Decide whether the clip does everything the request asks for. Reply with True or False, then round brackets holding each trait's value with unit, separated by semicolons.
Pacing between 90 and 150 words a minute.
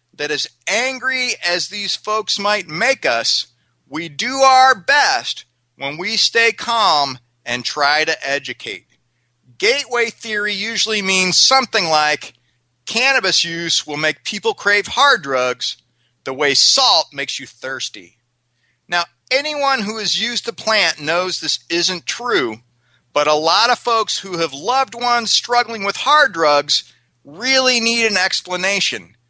True (140 wpm)